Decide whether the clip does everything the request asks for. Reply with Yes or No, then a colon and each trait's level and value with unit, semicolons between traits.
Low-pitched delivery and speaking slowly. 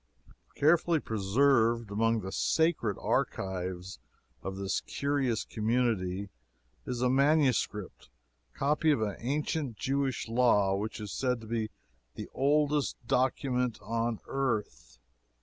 Yes: low, 120 Hz; slow, 115 wpm